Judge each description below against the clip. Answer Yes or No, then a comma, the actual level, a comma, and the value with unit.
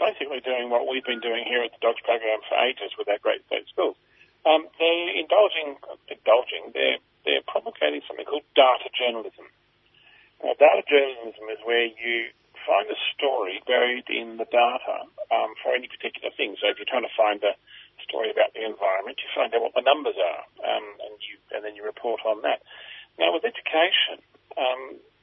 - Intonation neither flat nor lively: No, wide, 6.2 semitones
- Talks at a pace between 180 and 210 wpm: Yes, average, 185 wpm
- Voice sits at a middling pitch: No, low, 120 Hz